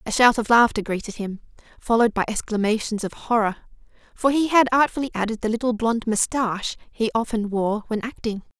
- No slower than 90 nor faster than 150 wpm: No, average, 175 wpm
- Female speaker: Yes, female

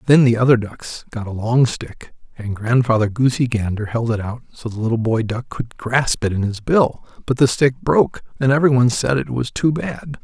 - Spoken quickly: Yes, fast, 225 wpm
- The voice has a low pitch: Yes, low, 120 Hz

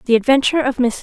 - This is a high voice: Yes, very high, 255 Hz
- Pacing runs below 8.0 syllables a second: No, 8.1 syllables/s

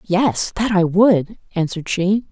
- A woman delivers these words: Yes, female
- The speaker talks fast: No, average, 155 wpm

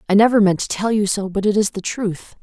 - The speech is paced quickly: Yes, fast, 295 wpm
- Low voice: No, high, 205 Hz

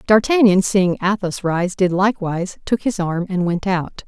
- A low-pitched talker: No, high, 190 Hz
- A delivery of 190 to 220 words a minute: No, average, 175 wpm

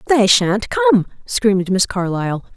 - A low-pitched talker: No, high, 220 Hz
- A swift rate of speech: No, average, 140 wpm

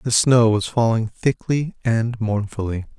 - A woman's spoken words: No, male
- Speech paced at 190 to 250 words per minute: No, average, 140 wpm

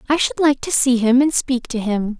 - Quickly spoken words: Yes, fast, 275 wpm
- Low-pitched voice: No, very high, 255 Hz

